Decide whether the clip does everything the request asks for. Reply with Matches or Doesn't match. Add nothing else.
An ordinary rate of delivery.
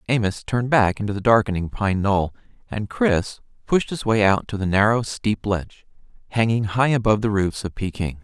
Matches